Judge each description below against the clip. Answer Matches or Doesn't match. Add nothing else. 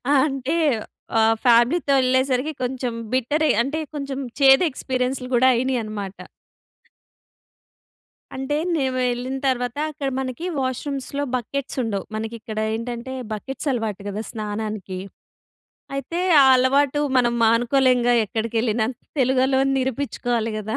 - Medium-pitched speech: Doesn't match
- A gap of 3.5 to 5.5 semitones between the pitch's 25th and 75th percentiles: Doesn't match